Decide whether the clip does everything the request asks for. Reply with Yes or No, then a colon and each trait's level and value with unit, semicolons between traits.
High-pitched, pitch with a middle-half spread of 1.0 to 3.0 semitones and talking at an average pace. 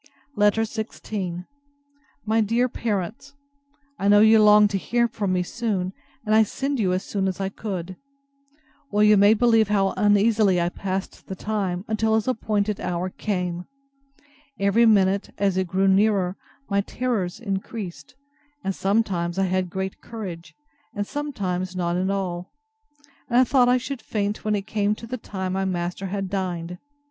Yes: high, 200 Hz; average, 2.7 semitones; average, 165 wpm